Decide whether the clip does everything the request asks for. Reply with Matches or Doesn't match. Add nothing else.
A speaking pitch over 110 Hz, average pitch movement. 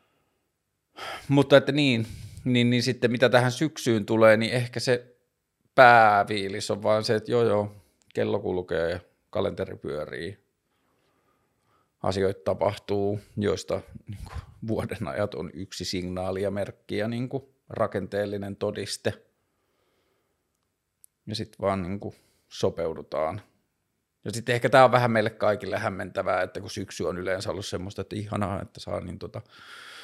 Doesn't match